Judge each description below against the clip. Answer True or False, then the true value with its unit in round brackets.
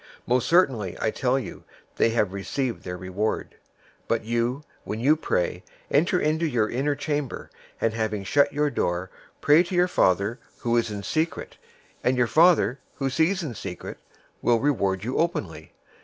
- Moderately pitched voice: False (125 Hz)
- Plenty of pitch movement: True (5.9 semitones)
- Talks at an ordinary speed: True (170 wpm)